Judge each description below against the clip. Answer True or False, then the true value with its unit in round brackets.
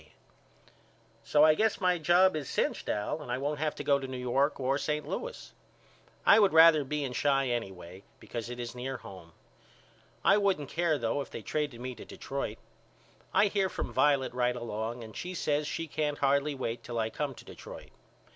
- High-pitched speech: False (140 Hz)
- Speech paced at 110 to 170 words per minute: False (200 wpm)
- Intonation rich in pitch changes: False (4.0 semitones)